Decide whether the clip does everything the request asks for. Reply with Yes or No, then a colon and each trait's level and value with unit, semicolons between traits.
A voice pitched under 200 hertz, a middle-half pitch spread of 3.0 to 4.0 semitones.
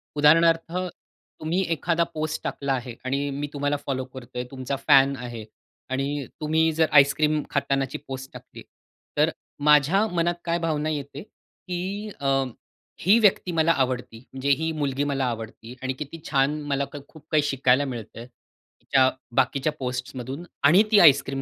Yes: medium, 140 Hz; average, 3.4 semitones